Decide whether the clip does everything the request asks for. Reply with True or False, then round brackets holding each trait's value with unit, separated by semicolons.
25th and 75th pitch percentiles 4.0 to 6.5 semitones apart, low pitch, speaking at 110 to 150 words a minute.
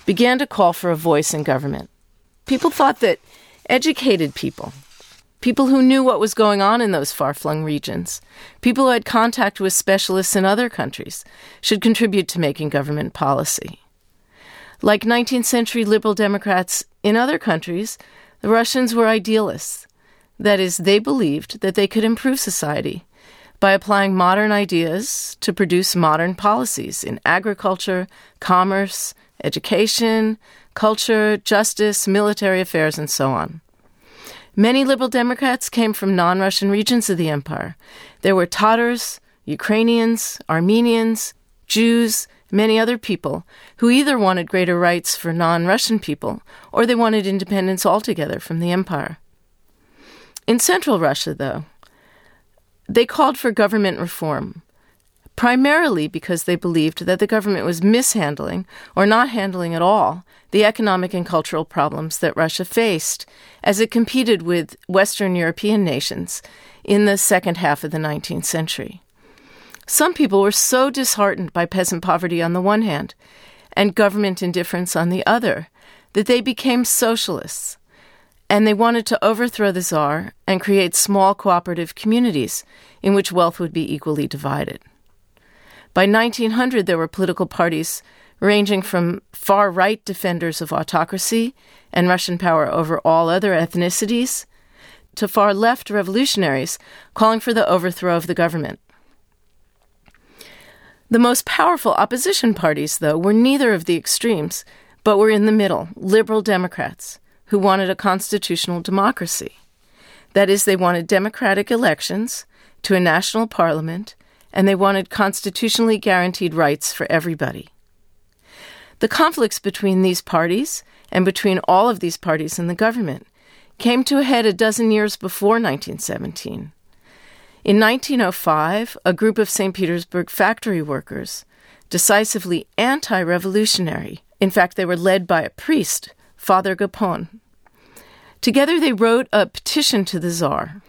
False (4.3 semitones; 200 Hz; 140 wpm)